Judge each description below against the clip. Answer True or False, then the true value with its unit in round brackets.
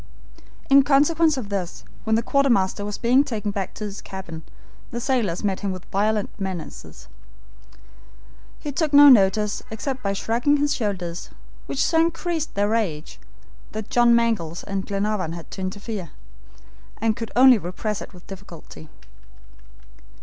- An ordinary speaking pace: True (150 wpm)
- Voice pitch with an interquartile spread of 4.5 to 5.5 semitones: True (4.9 semitones)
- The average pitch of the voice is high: True (210 Hz)